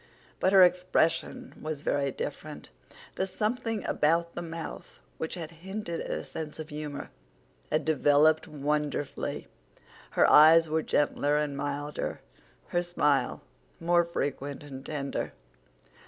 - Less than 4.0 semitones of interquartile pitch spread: Yes, average, 2.8 semitones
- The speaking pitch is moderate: Yes, medium, 155 Hz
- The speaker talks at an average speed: No, slow, 125 wpm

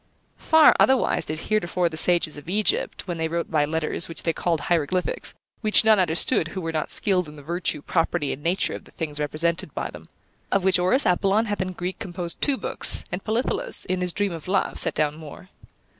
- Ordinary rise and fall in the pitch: Yes, average, 3.3 semitones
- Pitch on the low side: No, medium, 175 Hz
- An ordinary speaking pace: No, fast, 210 wpm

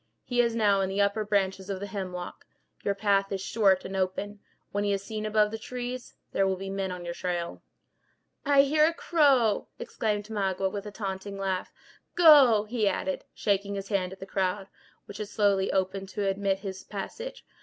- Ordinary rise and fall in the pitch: No, narrow, 2.0 semitones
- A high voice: Yes, high, 200 Hz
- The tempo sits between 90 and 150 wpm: No, average, 195 wpm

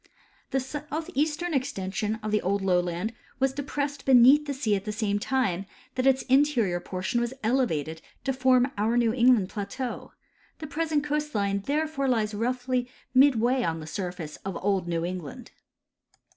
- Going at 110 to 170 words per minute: Yes, average, 160 wpm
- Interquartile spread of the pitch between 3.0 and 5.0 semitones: No, wide, 5.4 semitones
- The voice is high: Yes, high, 240 Hz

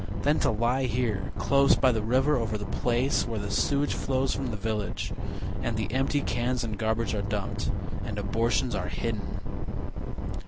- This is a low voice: Yes, low, 115 Hz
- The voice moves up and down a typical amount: Yes, average, 3.5 semitones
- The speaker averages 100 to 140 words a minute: No, average, 170 wpm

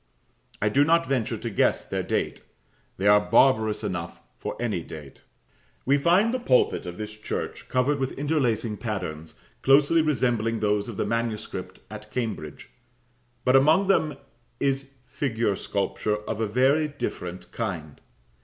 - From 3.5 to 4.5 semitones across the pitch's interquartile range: No, average, 5.0 semitones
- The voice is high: No, low, 115 Hz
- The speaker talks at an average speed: Yes, average, 145 wpm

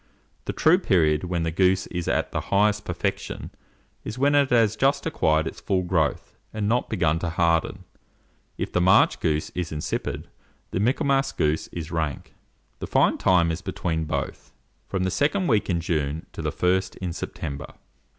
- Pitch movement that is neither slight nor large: Yes, average, 4.7 semitones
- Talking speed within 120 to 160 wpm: No, average, 175 wpm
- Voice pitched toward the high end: No, very low, 90 Hz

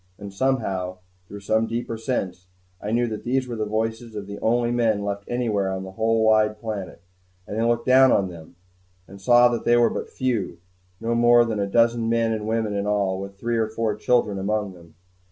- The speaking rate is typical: No, fast, 210 wpm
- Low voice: Yes, low, 110 Hz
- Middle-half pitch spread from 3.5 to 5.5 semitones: No, average, 2.8 semitones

